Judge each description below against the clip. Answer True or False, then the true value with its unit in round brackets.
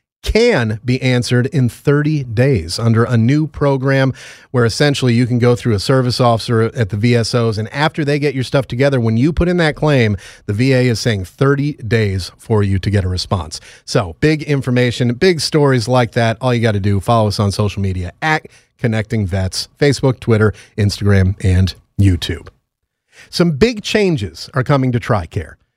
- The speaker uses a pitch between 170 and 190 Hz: False (120 Hz)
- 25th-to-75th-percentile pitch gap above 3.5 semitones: True (4.6 semitones)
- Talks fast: False (185 wpm)